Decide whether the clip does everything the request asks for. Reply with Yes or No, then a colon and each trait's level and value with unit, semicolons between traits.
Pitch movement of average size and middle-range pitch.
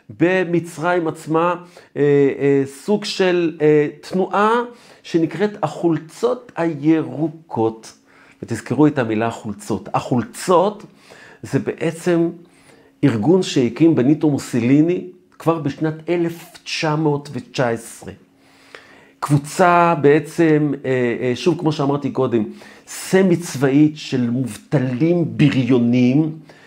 Yes: average, 4.4 semitones; medium, 150 Hz